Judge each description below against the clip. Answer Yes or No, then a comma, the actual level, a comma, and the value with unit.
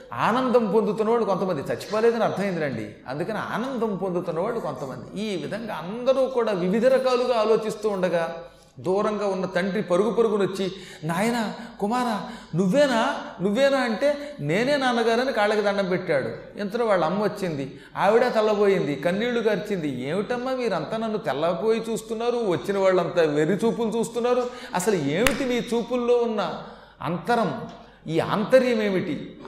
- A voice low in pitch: No, high, 215 Hz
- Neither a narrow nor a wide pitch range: Yes, average, 4.4 semitones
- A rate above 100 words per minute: Yes, average, 120 wpm